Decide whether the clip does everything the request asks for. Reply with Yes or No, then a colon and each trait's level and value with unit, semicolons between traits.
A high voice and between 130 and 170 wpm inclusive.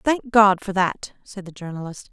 No: high, 195 Hz; average, 200 wpm